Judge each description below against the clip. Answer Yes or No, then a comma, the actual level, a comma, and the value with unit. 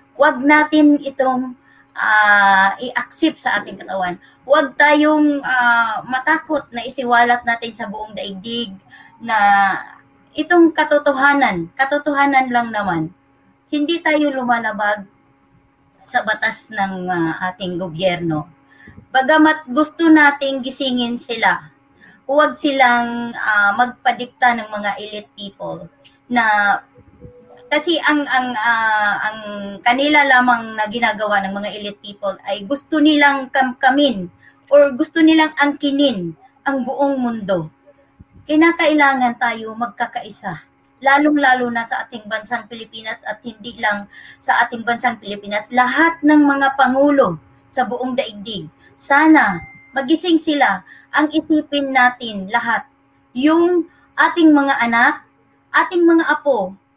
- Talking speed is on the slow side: Yes, slow, 115 wpm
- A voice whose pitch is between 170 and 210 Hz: No, high, 245 Hz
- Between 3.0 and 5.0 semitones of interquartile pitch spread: No, wide, 5.5 semitones